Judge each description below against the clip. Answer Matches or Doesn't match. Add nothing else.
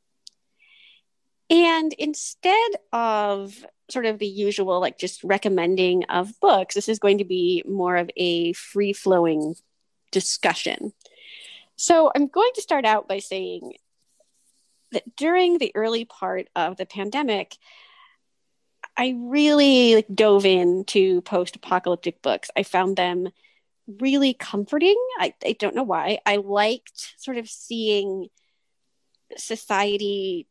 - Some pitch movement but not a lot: Doesn't match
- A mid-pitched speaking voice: Doesn't match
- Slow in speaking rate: Matches